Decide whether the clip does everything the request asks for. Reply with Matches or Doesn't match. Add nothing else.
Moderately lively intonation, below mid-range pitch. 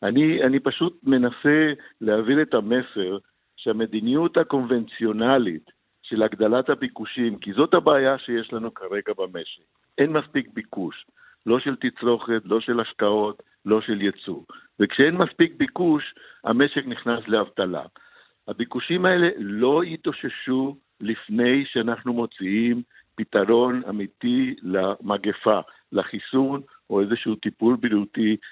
Matches